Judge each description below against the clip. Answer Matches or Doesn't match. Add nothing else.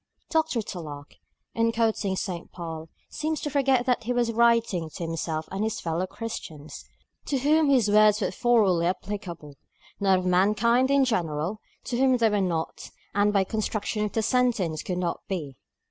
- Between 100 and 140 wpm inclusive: Doesn't match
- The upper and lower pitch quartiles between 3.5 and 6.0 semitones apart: Matches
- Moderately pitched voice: Doesn't match